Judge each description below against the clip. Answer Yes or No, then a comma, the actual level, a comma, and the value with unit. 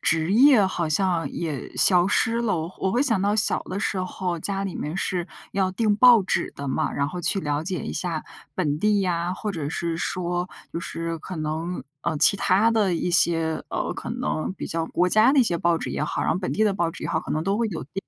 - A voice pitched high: No, medium, 180 Hz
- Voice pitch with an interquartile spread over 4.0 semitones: No, average, 3.4 semitones